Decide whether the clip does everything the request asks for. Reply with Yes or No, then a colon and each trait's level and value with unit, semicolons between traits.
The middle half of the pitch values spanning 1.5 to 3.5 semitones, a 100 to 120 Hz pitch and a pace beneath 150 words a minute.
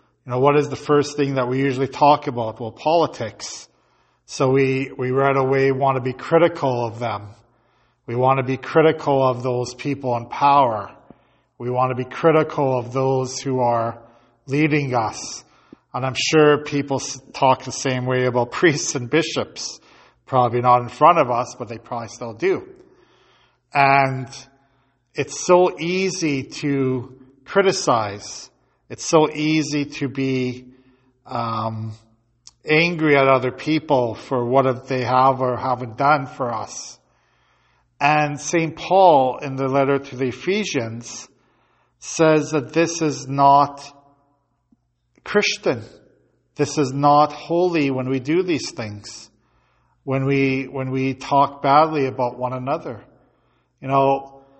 No: narrow, 2.5 semitones; low, 135 Hz; average, 140 wpm